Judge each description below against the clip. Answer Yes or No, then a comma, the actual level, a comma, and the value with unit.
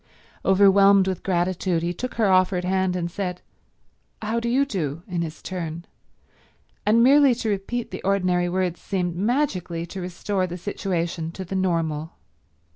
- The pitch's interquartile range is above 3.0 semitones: No, narrow, 2.5 semitones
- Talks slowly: No, average, 155 wpm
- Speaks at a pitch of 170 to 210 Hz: Yes, medium, 185 Hz